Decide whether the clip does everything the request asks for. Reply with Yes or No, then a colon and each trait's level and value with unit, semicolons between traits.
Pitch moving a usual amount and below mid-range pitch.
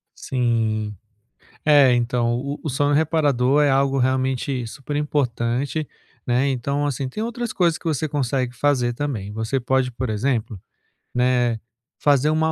Yes: average, 3.1 semitones; low, 130 Hz